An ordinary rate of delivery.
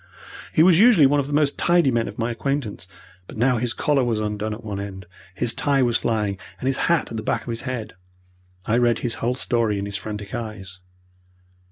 No: fast, 220 wpm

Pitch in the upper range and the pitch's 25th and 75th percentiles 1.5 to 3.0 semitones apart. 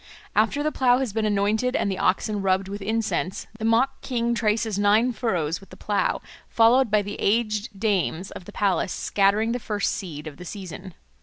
Yes: high, 210 Hz; average, 2.7 semitones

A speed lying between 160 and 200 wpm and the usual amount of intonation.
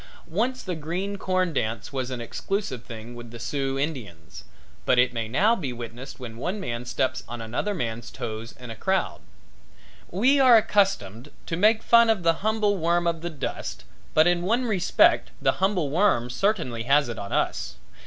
No: average, 185 wpm; wide, 8.5 semitones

